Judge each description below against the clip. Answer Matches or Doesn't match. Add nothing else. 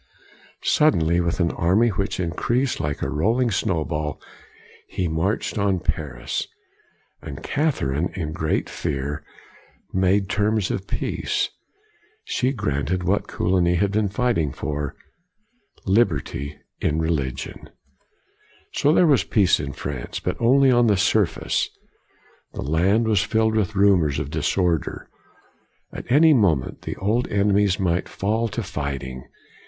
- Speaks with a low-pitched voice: Matches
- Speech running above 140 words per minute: Doesn't match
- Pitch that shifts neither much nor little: Doesn't match